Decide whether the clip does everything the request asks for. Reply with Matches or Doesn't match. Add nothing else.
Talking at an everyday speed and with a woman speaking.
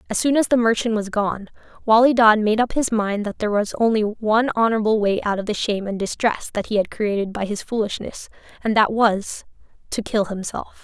Doesn't match